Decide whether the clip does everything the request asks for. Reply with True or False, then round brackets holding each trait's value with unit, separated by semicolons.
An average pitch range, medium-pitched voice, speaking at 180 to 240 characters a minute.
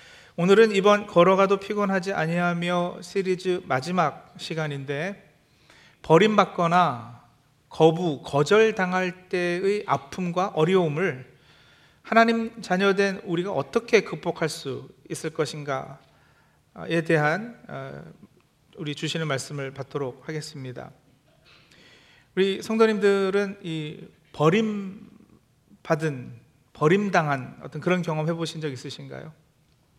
True (4.4 semitones; 175 Hz; 235 characters per minute)